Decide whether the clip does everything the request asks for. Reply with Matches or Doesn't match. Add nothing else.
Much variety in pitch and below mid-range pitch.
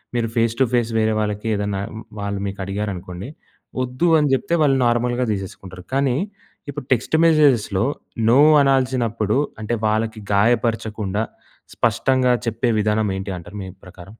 Doesn't match